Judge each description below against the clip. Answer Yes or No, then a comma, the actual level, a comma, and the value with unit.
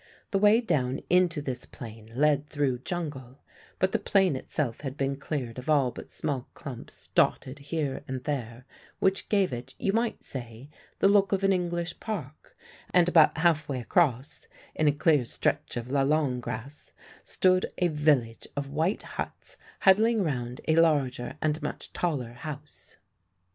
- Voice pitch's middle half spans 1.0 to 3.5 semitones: No, average, 5.1 semitones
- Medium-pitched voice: Yes, medium, 145 Hz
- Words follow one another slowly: No, average, 160 wpm